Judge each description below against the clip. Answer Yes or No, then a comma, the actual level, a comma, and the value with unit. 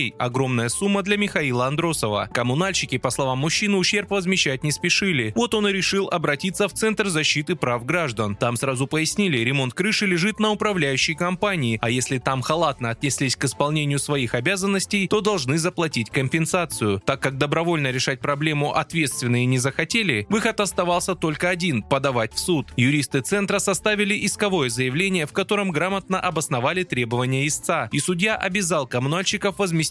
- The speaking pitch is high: No, medium, 160 Hz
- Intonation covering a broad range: Yes, wide, 6.4 semitones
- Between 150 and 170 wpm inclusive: Yes, average, 155 wpm